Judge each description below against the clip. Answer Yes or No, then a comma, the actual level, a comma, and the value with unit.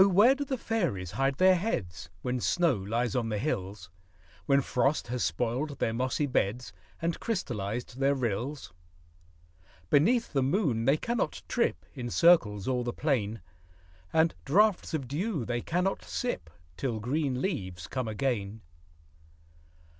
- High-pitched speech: No, low, 130 Hz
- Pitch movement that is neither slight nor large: No, wide, 6.7 semitones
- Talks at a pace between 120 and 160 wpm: Yes, average, 140 wpm